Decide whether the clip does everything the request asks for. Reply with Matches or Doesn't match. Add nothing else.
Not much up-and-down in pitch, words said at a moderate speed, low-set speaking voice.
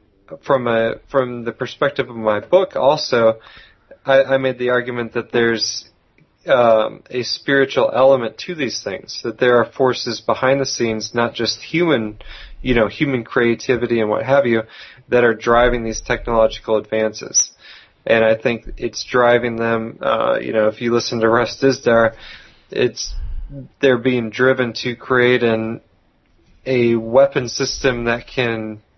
Matches